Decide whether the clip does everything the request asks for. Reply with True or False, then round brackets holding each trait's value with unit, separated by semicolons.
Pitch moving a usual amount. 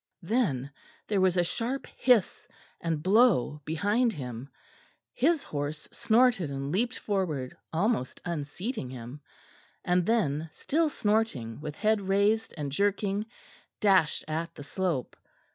False (6.8 semitones)